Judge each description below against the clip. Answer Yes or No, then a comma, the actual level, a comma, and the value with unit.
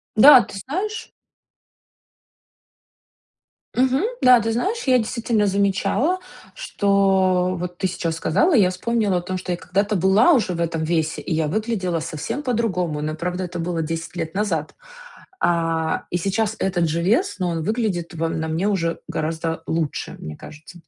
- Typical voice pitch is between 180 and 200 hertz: Yes, medium, 185 Hz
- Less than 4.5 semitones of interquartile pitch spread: No, average, 5.0 semitones